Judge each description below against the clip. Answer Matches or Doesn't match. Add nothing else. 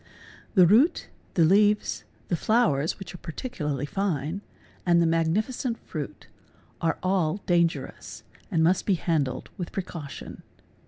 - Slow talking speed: Matches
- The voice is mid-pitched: Matches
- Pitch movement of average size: Matches